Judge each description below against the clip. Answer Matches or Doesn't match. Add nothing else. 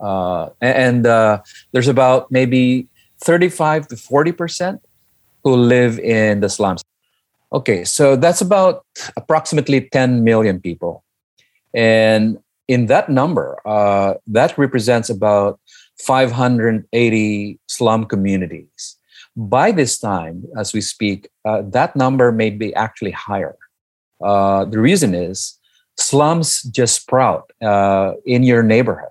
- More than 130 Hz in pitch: Doesn't match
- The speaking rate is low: Matches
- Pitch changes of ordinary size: Matches